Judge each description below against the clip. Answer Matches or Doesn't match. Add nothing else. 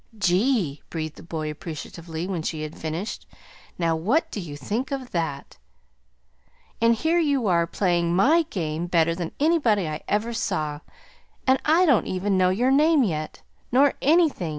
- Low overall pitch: Doesn't match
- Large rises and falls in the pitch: Matches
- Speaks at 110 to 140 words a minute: Doesn't match